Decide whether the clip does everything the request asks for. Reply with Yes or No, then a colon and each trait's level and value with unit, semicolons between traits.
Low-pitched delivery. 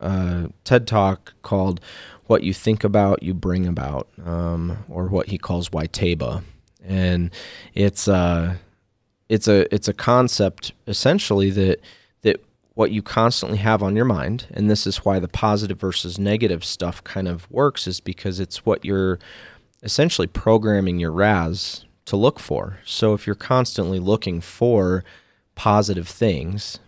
Yes: very low, 95 Hz